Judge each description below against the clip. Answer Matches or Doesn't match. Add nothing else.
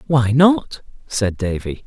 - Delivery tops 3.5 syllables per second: Doesn't match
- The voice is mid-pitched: Doesn't match